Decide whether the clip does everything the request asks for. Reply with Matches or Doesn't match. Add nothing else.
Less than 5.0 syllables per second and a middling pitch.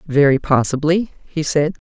Matches